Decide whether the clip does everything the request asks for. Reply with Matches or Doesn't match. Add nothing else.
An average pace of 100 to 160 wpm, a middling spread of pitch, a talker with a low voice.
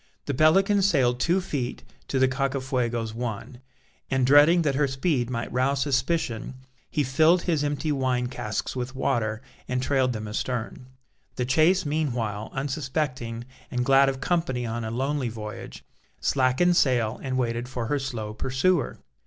Matches